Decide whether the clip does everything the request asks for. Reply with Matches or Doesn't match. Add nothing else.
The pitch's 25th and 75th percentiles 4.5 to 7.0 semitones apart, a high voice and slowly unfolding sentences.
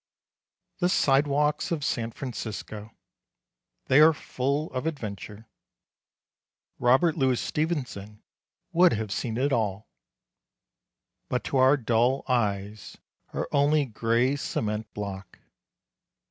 Doesn't match